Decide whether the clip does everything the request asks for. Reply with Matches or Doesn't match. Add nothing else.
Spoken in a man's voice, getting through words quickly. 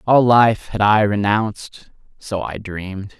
Doesn't match